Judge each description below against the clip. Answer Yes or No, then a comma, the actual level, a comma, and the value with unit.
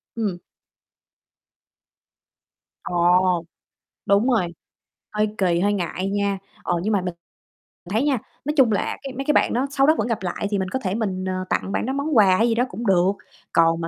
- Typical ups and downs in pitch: Yes, average, 4.3 semitones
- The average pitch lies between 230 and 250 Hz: No, high, 200 Hz